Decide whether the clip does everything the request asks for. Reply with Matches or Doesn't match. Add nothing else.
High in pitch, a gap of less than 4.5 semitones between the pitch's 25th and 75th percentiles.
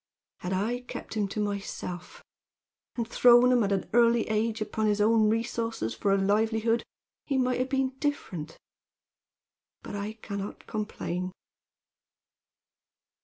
Matches